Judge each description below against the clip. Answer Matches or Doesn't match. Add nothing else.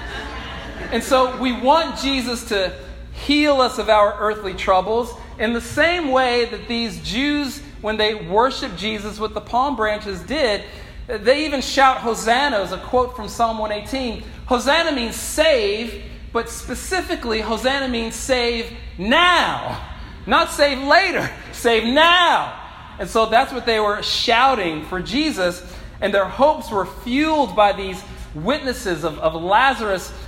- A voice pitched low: Doesn't match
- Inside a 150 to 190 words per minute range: Doesn't match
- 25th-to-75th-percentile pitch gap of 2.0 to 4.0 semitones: Doesn't match